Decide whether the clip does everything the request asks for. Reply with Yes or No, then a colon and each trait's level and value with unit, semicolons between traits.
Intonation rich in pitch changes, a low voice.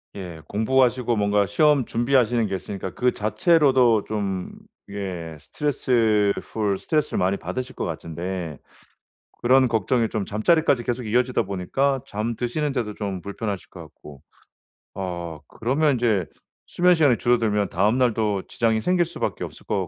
No: average, 4.5 semitones; low, 110 Hz